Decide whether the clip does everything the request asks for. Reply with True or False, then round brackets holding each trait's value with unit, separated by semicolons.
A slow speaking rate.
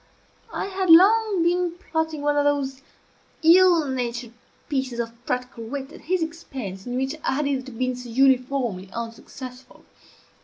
False (150 wpm)